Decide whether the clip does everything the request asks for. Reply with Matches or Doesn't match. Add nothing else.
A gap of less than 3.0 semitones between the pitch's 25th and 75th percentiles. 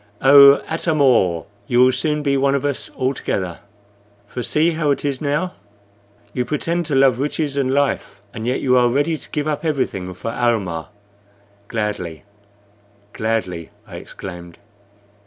Doesn't match